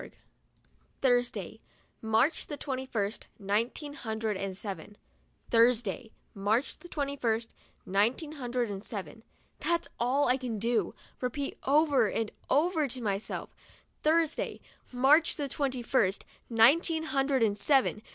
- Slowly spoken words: Yes, slow, 130 wpm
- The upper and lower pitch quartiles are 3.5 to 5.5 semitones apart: Yes, average, 4.4 semitones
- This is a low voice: No, high, 245 Hz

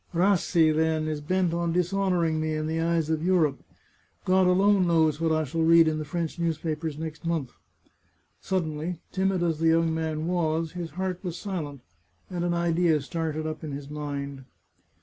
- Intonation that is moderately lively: No, narrow, 2.0 semitones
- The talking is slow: No, average, 175 wpm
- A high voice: No, medium, 165 Hz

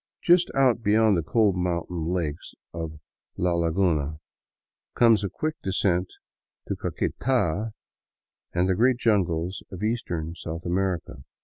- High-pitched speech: No, very low, 90 Hz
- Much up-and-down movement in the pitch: No, average, 4.7 semitones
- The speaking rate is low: Yes, slow, 125 wpm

